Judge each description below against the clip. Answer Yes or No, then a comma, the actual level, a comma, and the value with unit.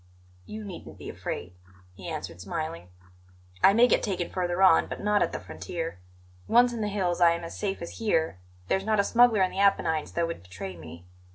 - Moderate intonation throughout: Yes, average, 4.7 semitones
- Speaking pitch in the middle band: Yes, medium, 175 Hz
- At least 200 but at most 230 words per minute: Yes, fast, 205 wpm